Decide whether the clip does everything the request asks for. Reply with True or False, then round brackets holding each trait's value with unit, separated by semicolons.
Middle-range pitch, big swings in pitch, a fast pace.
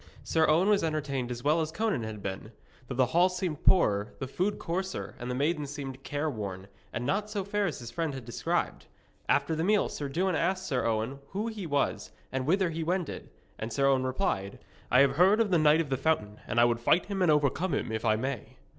True (145 Hz; 6.4 semitones; 225 wpm)